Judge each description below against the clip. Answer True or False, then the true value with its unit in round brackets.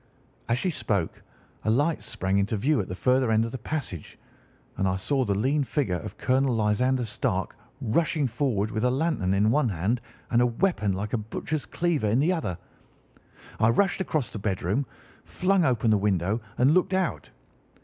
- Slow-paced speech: False (185 wpm)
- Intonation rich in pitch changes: True (5.9 semitones)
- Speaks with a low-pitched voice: True (120 Hz)